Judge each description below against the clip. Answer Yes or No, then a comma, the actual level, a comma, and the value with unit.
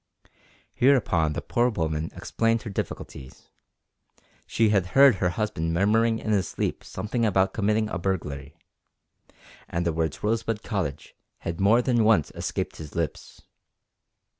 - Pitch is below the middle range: Yes, low, 100 Hz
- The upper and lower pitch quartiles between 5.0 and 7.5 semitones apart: Yes, wide, 5.4 semitones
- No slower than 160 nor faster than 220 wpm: No, average, 140 wpm